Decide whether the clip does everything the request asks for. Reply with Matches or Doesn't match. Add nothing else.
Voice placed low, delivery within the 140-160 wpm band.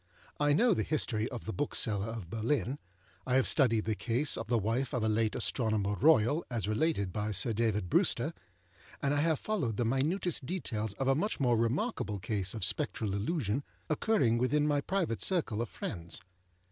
Doesn't match